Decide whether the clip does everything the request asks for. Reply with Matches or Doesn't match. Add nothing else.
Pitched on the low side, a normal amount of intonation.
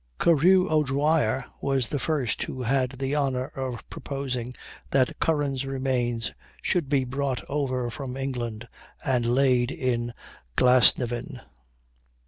Doesn't match